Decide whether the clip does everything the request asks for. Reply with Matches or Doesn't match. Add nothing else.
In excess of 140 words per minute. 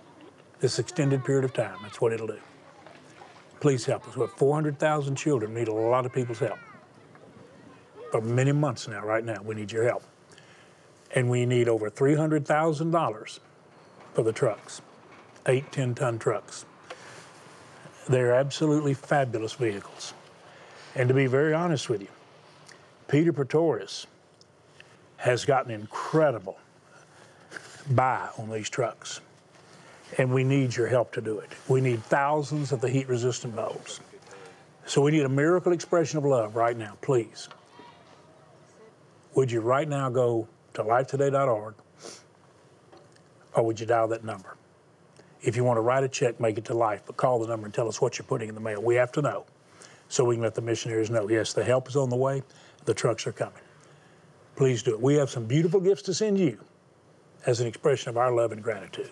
Matches